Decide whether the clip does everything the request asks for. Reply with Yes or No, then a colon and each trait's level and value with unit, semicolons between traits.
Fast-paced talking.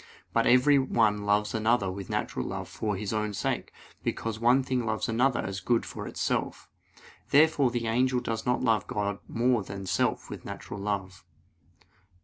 No: average, 165 wpm